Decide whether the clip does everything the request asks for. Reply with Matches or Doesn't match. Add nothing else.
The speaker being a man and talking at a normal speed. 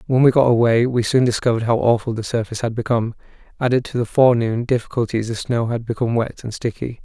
Doesn't match